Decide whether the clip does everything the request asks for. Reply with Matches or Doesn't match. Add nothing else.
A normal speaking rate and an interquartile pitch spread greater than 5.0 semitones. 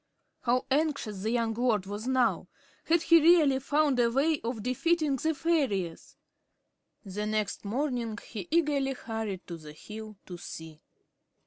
Matches